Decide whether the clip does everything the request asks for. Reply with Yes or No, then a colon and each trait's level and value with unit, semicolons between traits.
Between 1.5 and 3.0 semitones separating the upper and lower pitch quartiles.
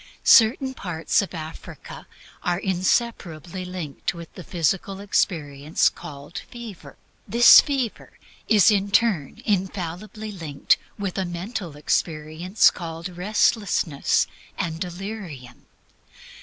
No: average, 4.0 semitones